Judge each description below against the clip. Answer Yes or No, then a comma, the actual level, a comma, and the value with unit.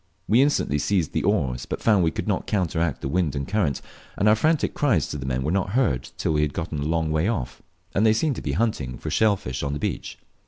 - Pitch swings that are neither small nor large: No, wide, 7.0 semitones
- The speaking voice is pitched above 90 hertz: No, very low, 85 Hz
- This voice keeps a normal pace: No, fast, 260 wpm